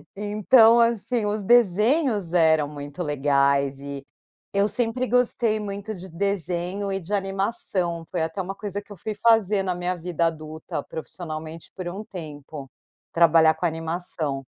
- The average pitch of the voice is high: No, medium, 180 Hz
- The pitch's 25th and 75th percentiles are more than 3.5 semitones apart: Yes, average, 4.5 semitones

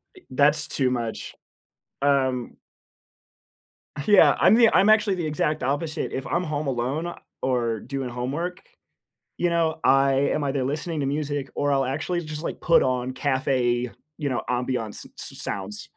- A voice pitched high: No, medium, 140 Hz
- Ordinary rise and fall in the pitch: Yes, average, 3.4 semitones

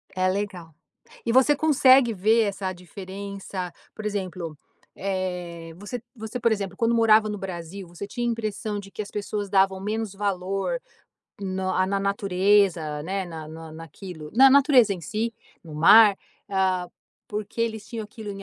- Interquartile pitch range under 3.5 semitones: Yes, average, 2.9 semitones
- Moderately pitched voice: No, high, 200 Hz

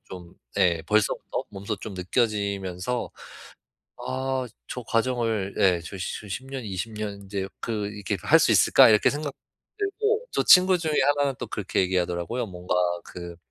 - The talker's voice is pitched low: Yes, low, 105 Hz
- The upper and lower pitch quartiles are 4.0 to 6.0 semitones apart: Yes, average, 5.2 semitones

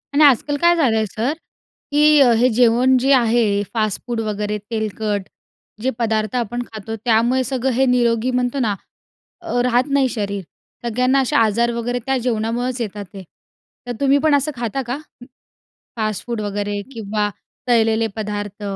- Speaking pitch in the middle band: No, high, 235 Hz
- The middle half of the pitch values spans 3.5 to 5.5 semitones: No, average, 3.0 semitones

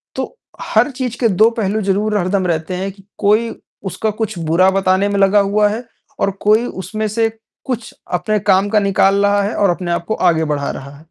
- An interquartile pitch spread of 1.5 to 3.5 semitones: Yes, narrow, 2.5 semitones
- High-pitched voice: Yes, high, 200 Hz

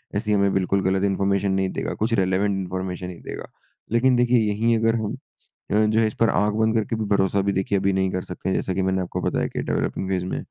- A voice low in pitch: Yes, low, 100 Hz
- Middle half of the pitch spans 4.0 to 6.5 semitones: No, narrow, 2.4 semitones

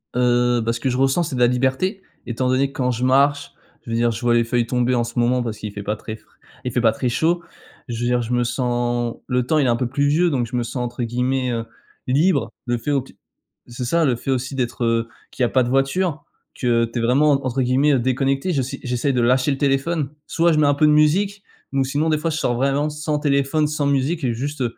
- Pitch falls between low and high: No, low, 130 Hz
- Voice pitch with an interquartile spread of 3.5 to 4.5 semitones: No, average, 3.0 semitones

